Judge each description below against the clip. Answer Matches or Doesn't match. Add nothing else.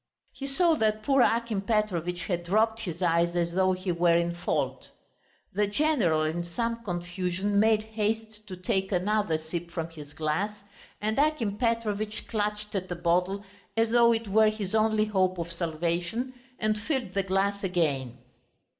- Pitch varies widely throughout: Doesn't match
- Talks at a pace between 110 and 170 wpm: Matches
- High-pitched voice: Matches